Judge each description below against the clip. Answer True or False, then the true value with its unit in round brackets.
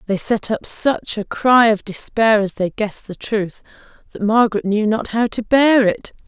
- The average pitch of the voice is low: False (215 Hz)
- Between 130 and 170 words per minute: False (200 wpm)